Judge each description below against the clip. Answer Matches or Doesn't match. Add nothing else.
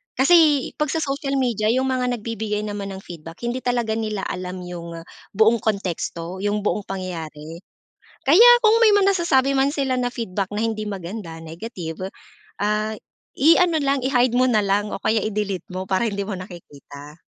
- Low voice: Doesn't match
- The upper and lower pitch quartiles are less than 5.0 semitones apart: Doesn't match